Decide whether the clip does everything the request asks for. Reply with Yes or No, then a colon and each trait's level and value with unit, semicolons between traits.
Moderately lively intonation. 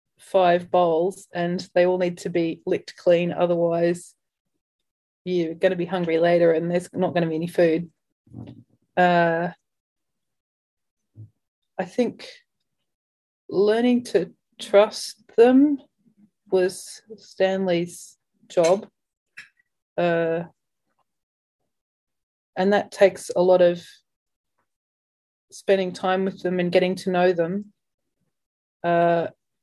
No: narrow, 2.3 semitones